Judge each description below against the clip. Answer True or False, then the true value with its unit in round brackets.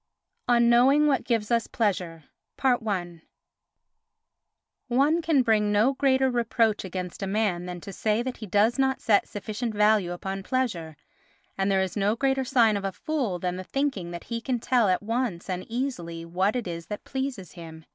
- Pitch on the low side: False (215 Hz)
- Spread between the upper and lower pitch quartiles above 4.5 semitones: True (5.1 semitones)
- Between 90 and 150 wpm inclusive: False (180 wpm)